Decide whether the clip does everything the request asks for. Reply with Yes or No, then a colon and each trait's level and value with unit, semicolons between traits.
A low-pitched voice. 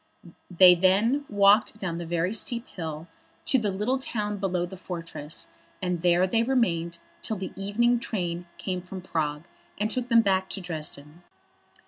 No: high, 190 Hz